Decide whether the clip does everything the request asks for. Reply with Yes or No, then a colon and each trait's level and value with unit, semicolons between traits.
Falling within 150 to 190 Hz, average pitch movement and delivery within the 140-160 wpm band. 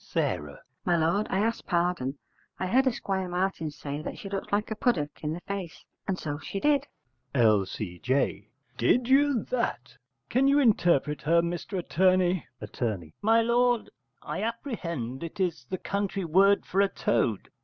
No: medium, 185 Hz; wide, 6.1 semitones; average, 155 wpm